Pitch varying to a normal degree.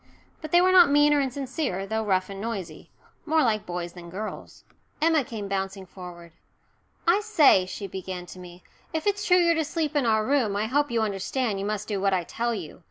No: wide, 7.5 semitones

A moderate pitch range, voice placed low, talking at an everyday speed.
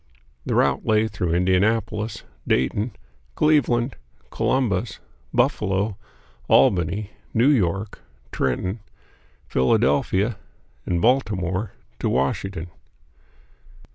No: average, 3.7 semitones; low, 100 Hz; slow, 75 wpm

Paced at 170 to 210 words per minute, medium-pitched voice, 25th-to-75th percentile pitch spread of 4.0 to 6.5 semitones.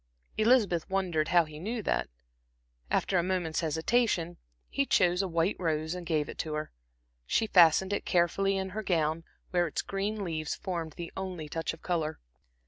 No: average, 175 wpm; medium, 175 Hz; average, 3.1 semitones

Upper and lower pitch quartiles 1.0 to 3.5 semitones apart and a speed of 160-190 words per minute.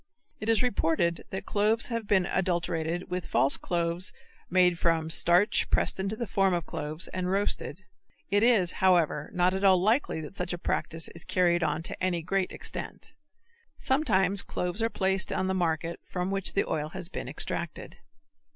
Yes: narrow, 2.5 semitones; average, 175 wpm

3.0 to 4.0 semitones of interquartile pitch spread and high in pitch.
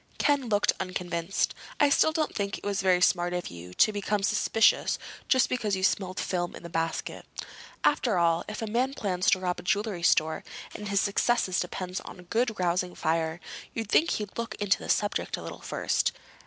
Yes: average, 3.4 semitones; high, 195 Hz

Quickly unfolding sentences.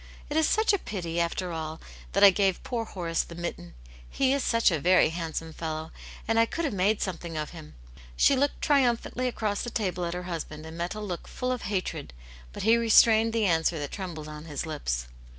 Yes: fast, 220 wpm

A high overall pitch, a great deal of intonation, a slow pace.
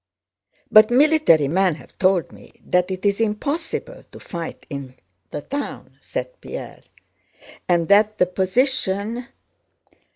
Yes: high, 200 Hz; wide, 6.1 semitones; slow, 125 wpm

